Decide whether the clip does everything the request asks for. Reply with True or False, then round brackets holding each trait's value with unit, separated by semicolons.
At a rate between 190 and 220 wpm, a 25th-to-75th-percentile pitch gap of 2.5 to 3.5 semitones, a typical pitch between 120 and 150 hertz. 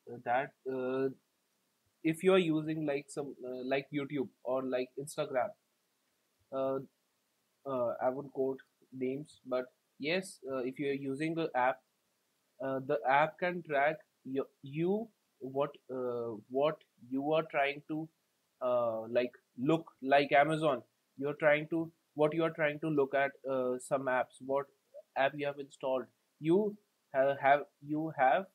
False (155 wpm; 3.1 semitones; 140 Hz)